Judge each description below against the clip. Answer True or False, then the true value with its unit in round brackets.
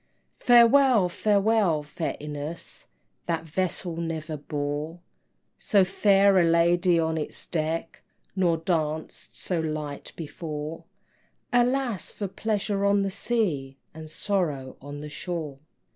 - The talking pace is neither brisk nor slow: False (115 wpm)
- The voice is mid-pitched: True (170 Hz)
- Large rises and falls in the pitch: False (4.3 semitones)